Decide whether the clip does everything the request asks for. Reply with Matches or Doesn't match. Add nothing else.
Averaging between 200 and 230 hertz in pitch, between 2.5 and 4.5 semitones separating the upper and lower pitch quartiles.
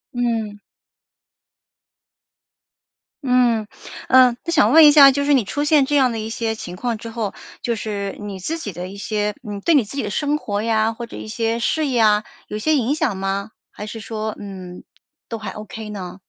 Matches